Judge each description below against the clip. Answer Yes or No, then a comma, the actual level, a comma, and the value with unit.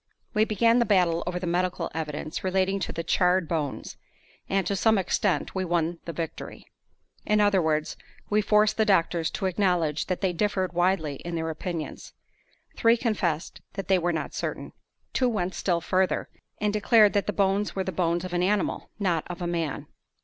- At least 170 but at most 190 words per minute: Yes, average, 185 wpm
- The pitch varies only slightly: No, average, 3.1 semitones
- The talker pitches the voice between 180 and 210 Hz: Yes, medium, 185 Hz